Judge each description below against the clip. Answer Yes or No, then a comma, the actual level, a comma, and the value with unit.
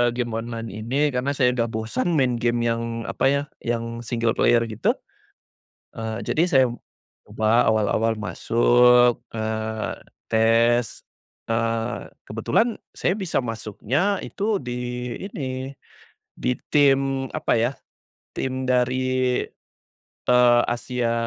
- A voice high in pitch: No, low, 120 Hz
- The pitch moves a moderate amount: No, narrow, 2.1 semitones